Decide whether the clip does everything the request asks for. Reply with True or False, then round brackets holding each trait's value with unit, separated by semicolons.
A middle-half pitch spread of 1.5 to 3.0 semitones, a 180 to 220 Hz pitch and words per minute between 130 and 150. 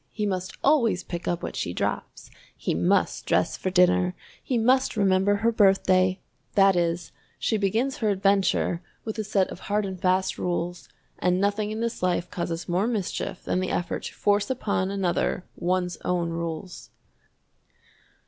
False (2.7 semitones; 190 Hz; 165 wpm)